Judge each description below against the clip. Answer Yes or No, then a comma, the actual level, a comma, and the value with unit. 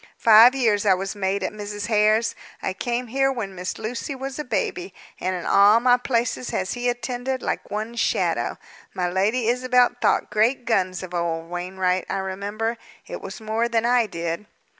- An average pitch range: Yes, average, 4.3 semitones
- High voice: Yes, high, 215 Hz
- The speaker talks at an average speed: Yes, average, 180 wpm